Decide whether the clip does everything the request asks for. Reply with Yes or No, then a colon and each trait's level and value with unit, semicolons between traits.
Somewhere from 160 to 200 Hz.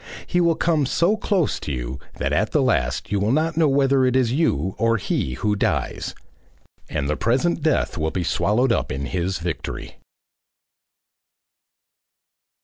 No: low, 115 Hz